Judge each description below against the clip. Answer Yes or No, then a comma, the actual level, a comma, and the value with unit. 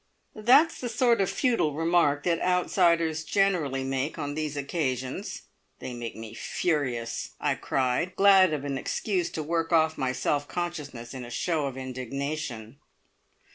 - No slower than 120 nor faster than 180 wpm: Yes, average, 150 wpm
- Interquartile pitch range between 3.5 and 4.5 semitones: No, average, 4.9 semitones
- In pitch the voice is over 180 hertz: No, medium, 150 Hz